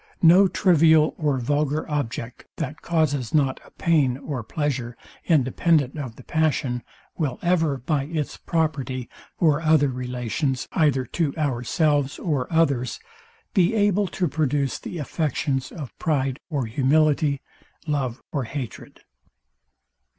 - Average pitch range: Yes, average, 3.4 semitones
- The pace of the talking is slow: Yes, slow, 125 wpm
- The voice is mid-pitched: Yes, medium, 145 Hz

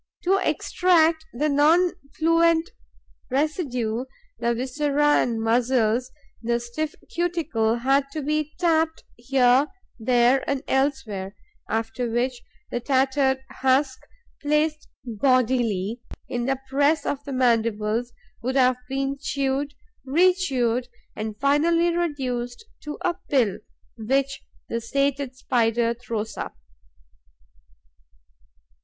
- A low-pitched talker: No, very high, 265 Hz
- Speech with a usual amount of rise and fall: Yes, average, 3.8 semitones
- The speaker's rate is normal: No, slow, 105 wpm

